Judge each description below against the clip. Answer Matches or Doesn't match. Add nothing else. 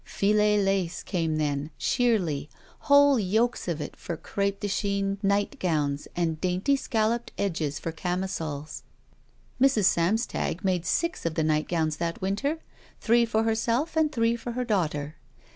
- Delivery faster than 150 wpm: Doesn't match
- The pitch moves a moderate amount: Doesn't match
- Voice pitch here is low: Doesn't match